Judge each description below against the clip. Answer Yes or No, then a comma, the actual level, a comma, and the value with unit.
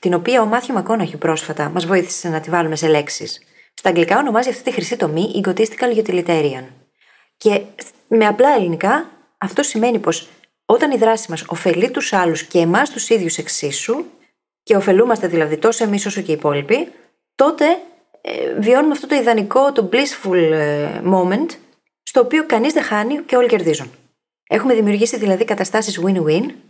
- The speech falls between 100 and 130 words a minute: No, average, 165 wpm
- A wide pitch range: Yes, wide, 6.4 semitones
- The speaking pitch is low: No, high, 205 Hz